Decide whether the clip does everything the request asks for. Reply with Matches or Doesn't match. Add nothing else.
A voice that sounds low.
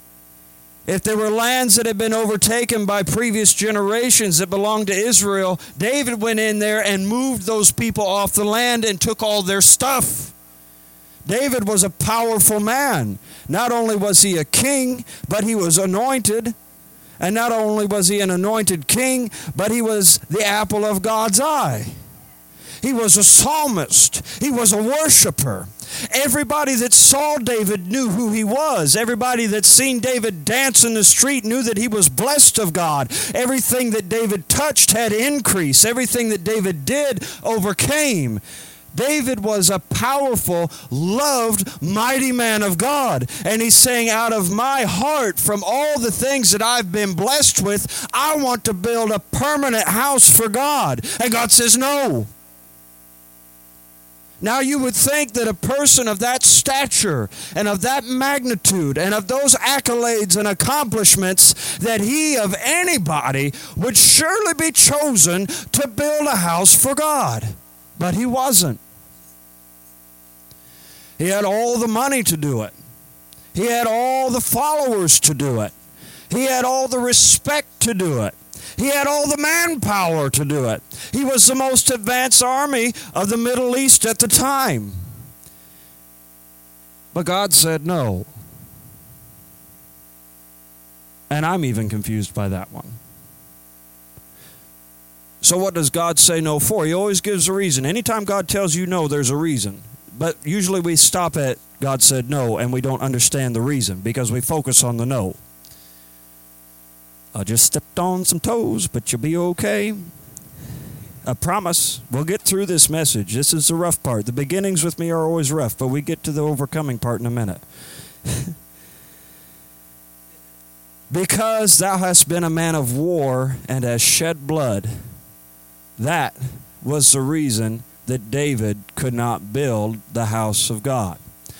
Doesn't match